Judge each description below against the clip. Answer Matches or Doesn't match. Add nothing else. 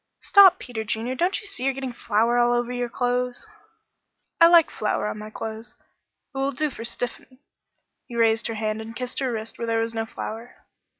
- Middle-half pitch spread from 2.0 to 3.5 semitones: Matches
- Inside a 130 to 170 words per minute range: Doesn't match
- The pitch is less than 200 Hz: Doesn't match